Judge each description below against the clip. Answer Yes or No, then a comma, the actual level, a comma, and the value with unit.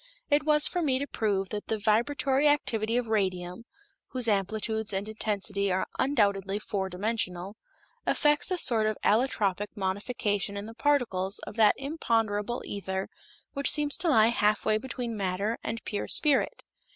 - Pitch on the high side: Yes, high, 220 Hz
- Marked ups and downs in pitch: No, average, 4.2 semitones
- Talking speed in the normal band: Yes, average, 150 wpm